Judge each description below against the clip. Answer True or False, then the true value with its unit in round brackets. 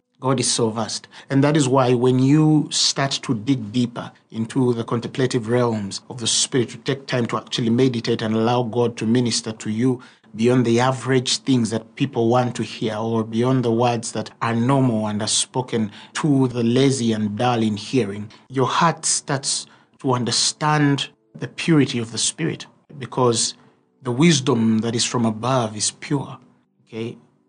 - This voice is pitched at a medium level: False (120 Hz)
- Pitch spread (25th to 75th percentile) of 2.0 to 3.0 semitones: True (2.6 semitones)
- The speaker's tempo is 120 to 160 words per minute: False (175 wpm)